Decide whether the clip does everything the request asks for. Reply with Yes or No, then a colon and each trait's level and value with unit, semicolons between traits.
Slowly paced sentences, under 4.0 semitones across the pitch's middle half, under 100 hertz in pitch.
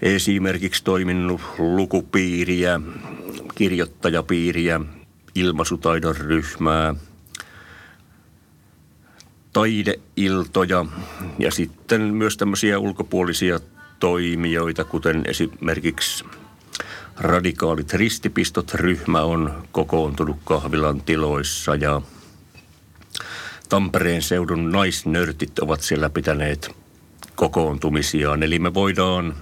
Yes: slow, 65 wpm; average, 2.8 semitones; very low, 85 Hz